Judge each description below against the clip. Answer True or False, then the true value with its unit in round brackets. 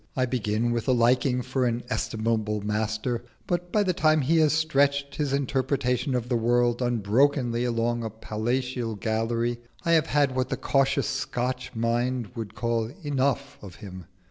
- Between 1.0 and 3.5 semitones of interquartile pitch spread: True (3.1 semitones)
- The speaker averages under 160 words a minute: False (165 wpm)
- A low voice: True (120 Hz)